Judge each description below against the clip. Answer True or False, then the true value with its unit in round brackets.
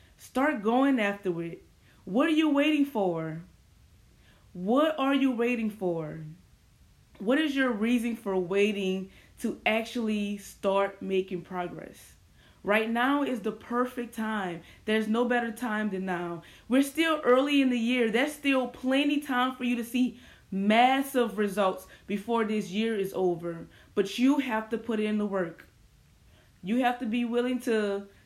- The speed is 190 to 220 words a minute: False (155 wpm)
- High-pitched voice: True (225 Hz)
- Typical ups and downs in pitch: True (4.5 semitones)